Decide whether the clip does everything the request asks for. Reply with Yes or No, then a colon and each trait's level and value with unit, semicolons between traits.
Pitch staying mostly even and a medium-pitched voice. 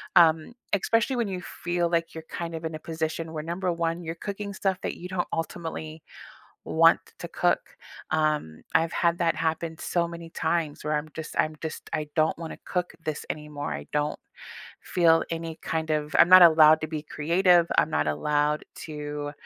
Yes: narrow, 1.8 semitones; medium, 165 Hz